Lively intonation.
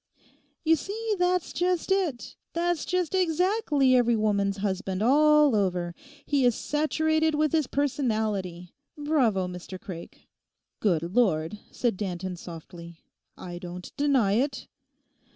Yes: wide, 8.7 semitones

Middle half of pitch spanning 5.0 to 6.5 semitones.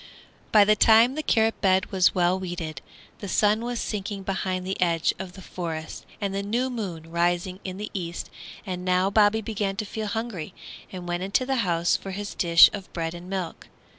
No: average, 3.2 semitones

